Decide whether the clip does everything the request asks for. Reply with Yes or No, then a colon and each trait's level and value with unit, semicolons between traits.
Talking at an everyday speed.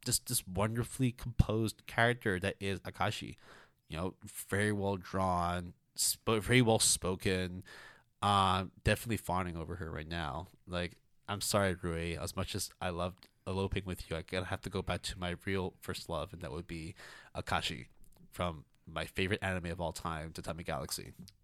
Yes: average, 175 wpm